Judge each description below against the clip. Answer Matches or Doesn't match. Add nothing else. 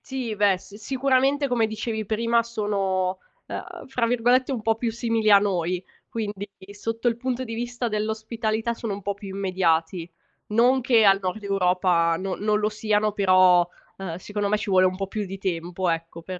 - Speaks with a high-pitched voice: Matches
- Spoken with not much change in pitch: Doesn't match